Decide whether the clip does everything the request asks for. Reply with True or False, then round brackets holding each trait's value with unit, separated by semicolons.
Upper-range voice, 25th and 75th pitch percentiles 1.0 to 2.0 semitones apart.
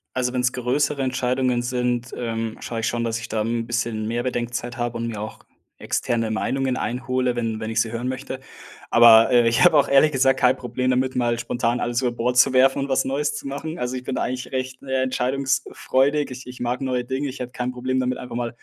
False (125 Hz; 1.7 semitones)